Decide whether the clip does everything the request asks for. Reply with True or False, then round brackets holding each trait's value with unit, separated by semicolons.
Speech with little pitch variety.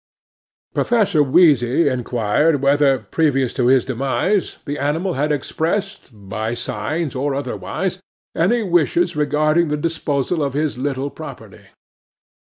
False (4.1 semitones)